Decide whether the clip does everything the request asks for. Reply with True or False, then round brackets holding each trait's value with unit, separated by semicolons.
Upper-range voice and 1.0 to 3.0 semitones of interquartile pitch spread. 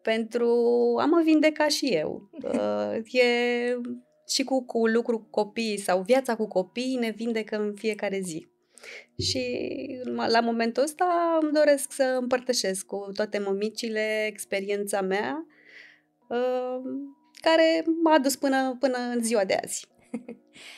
False (240 Hz; 4.3 semitones)